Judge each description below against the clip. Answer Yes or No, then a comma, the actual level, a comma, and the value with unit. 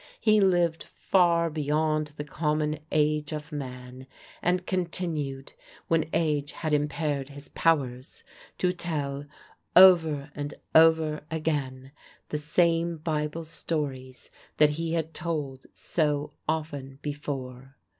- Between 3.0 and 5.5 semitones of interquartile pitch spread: No, narrow, 2.4 semitones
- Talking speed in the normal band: No, slow, 115 wpm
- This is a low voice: No, medium, 150 Hz